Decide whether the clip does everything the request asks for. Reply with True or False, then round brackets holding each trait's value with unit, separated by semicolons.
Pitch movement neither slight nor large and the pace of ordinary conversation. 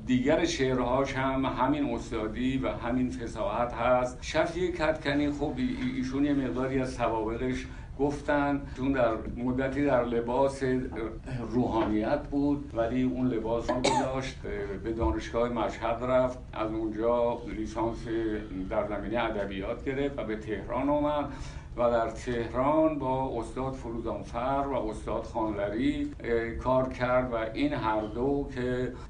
True (3.0 semitones; 130 wpm)